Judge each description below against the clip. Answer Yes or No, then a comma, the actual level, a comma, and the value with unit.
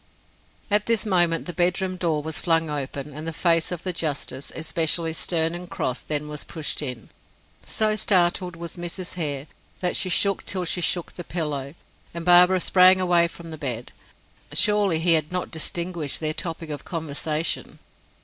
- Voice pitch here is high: No, medium, 165 Hz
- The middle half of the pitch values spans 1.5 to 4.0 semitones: Yes, average, 2.7 semitones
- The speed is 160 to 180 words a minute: Yes, average, 170 wpm